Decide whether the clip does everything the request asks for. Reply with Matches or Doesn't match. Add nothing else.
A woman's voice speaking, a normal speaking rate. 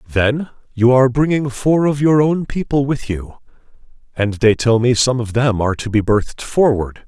Doesn't match